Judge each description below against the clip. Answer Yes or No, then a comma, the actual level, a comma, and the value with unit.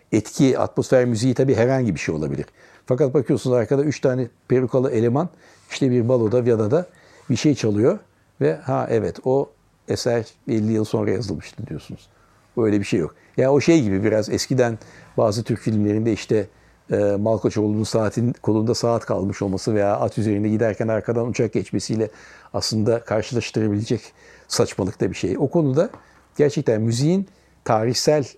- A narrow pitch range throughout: No, average, 3.1 semitones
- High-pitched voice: No, low, 115 Hz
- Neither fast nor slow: No, fast, 150 wpm